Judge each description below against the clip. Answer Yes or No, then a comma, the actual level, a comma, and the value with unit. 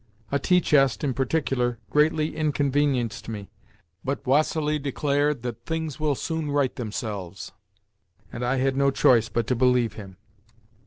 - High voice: No, low, 135 Hz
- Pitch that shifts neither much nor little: Yes, average, 3.6 semitones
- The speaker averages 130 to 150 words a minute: Yes, average, 145 wpm